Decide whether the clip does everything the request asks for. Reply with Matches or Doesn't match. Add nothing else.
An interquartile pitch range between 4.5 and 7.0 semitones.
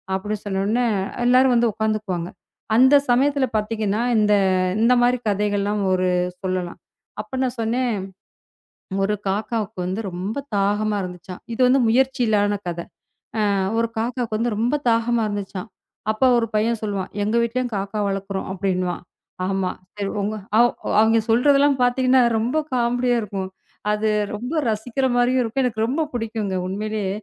Doesn't match